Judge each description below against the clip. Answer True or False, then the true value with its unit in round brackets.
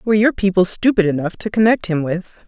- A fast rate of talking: True (220 wpm)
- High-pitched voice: True (195 Hz)